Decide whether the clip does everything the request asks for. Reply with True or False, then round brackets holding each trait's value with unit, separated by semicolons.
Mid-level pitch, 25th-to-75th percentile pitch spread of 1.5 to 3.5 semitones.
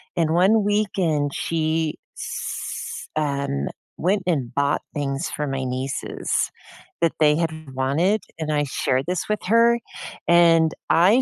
False (160 Hz; 4.2 semitones)